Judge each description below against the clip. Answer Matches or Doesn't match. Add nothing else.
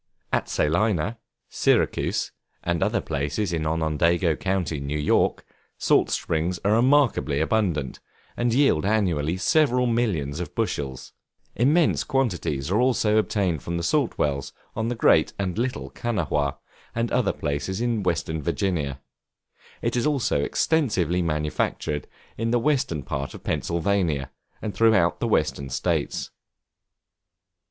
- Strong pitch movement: Matches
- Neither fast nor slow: Doesn't match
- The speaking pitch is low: Matches